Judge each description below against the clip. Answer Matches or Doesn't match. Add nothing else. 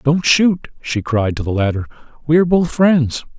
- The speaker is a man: Matches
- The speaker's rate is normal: Matches